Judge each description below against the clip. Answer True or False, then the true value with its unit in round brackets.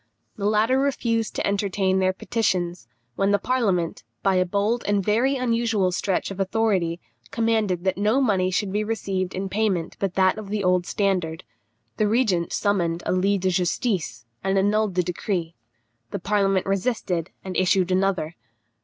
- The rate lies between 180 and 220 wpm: False (160 wpm)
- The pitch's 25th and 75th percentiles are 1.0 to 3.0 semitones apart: True (2.6 semitones)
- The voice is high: True (195 Hz)